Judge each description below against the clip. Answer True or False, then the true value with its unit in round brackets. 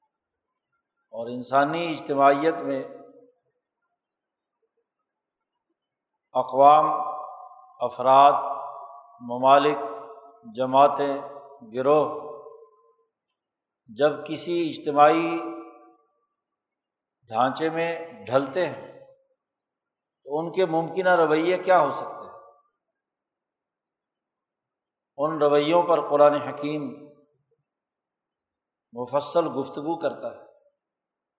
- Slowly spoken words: True (65 wpm)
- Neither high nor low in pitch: True (155 Hz)